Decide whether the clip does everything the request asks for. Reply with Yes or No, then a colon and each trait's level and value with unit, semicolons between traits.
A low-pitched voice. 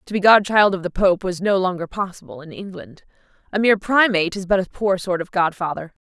No: high, 190 Hz